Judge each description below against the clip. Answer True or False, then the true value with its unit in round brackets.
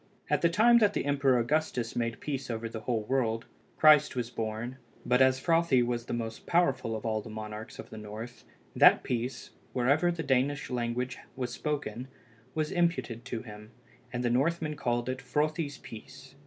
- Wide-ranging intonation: False (4.2 semitones)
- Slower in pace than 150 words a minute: False (180 wpm)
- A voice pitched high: False (125 Hz)